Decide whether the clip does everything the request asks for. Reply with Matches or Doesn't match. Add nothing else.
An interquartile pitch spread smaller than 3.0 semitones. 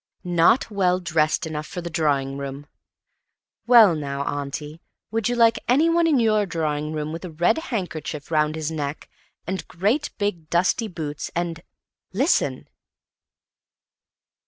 Doesn't match